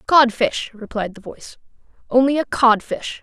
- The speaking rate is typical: Yes, average, 150 wpm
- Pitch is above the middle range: Yes, high, 240 Hz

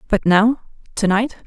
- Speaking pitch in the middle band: No, high, 215 Hz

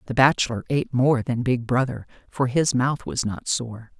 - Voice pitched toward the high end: No, low, 125 Hz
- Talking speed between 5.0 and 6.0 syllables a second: No, 4.8 syllables/s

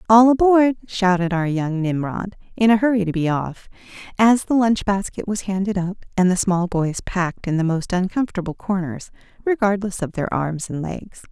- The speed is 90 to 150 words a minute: No, average, 185 wpm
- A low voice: No, high, 195 Hz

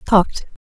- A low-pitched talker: No, high, 195 Hz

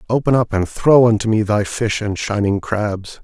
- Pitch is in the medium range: No, low, 110 Hz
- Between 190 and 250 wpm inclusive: Yes, fast, 205 wpm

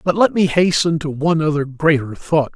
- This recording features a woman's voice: No, male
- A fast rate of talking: Yes, fast, 210 wpm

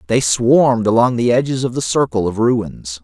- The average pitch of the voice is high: No, low, 115 Hz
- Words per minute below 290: Yes, average, 200 wpm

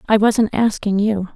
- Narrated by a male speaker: No, female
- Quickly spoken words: No, average, 175 wpm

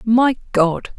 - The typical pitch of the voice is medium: No, high, 220 Hz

